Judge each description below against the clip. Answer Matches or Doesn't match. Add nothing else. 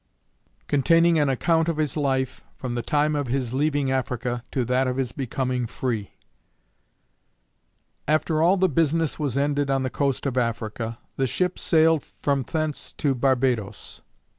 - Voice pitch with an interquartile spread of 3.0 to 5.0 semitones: Matches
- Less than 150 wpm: Doesn't match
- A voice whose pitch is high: Doesn't match